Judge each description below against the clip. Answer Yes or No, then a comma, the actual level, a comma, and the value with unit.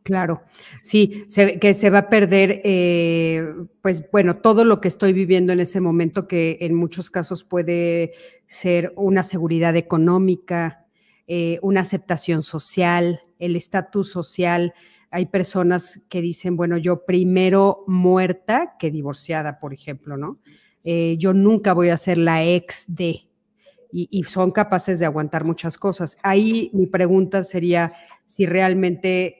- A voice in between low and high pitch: Yes, medium, 180 Hz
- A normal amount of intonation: No, narrow, 2.1 semitones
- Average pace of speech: Yes, average, 145 wpm